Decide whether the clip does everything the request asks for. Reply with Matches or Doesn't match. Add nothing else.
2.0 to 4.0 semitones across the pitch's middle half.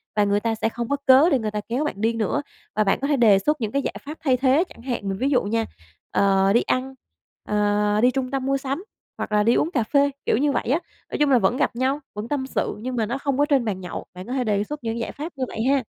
Doesn't match